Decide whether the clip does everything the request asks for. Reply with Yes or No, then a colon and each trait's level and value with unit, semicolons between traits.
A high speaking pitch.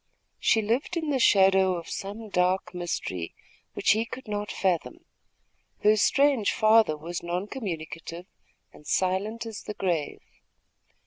Yes: high, 195 Hz